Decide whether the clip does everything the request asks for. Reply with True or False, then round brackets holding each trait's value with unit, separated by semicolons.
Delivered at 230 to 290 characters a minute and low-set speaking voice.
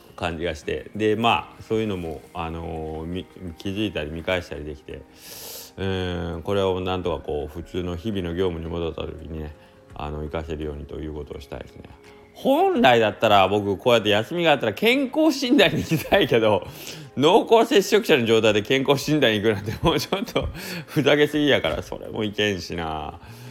False (375 characters per minute; 95 Hz)